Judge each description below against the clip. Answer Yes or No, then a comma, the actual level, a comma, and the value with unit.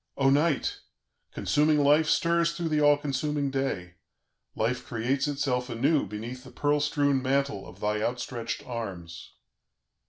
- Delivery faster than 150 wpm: No, slow, 135 wpm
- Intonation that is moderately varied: Yes, average, 3.9 semitones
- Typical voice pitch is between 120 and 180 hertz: Yes, low, 135 Hz